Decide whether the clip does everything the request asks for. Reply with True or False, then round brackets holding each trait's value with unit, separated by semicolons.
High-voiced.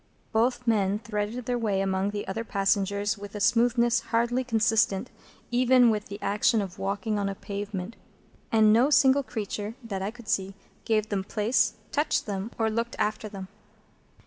True (215 Hz)